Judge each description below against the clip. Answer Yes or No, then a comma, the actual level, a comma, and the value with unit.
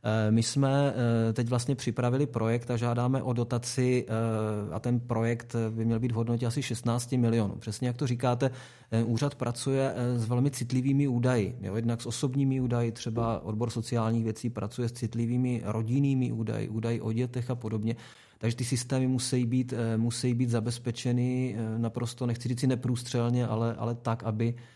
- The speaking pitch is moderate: No, low, 120 Hz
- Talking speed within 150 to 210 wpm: Yes, average, 160 wpm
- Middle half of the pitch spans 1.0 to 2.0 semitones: Yes, narrow, 1.7 semitones